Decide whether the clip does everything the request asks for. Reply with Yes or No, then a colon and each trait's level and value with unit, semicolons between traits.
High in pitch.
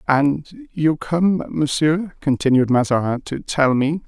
No: medium, 150 Hz